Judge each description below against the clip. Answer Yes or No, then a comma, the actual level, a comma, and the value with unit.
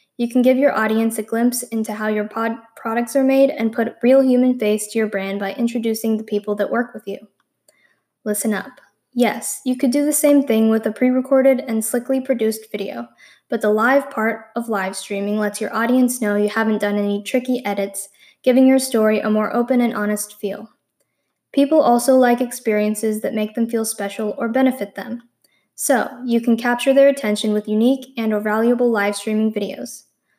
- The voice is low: No, high, 225 Hz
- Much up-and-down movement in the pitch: No, average, 3.1 semitones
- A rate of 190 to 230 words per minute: Yes, average, 195 wpm